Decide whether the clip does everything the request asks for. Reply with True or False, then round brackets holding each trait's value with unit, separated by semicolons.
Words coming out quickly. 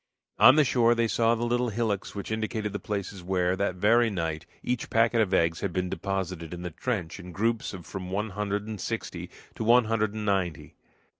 True (210 wpm)